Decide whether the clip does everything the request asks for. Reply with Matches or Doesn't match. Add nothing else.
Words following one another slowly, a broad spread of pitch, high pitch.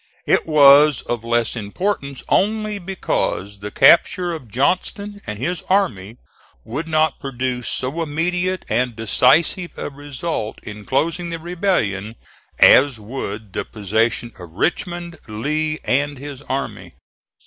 Doesn't match